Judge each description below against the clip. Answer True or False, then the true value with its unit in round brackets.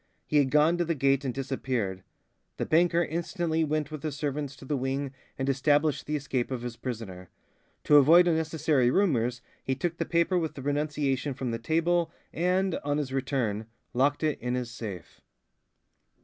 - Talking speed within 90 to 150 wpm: False (175 wpm)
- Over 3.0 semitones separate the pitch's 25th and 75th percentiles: True (3.7 semitones)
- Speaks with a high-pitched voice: False (145 Hz)